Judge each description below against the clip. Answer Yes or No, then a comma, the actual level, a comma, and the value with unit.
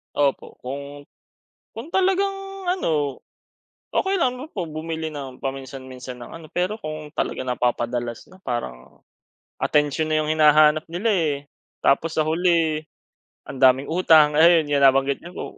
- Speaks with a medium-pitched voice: Yes, medium, 155 Hz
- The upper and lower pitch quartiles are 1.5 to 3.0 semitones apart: No, average, 3.6 semitones